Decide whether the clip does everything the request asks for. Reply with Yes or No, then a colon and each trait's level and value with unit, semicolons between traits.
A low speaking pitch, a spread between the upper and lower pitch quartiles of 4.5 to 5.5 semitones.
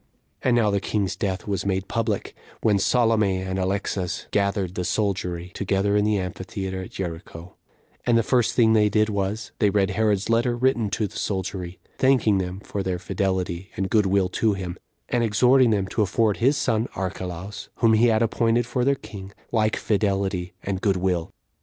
No: low, 100 Hz; average, 2.9 semitones